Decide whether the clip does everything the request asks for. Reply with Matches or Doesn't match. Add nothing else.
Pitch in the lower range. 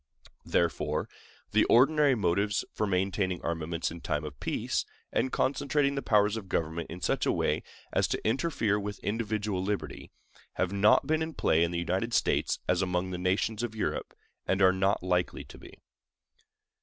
Matches